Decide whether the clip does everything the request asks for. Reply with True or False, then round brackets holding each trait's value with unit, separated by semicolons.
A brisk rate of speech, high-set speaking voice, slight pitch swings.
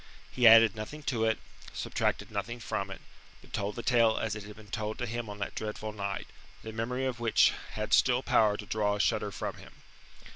False (215 wpm; 110 Hz; 2.1 semitones)